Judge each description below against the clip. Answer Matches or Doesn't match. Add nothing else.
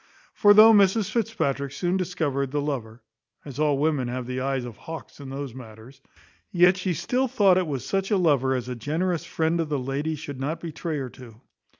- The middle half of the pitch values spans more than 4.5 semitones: Matches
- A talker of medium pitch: Matches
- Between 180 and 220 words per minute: Matches